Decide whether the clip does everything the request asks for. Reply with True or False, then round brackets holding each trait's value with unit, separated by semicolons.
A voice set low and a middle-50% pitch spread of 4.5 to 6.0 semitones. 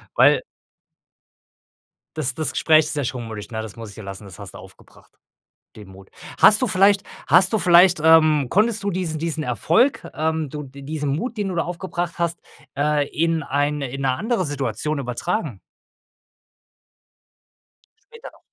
False (155 Hz; 5.0 semitones)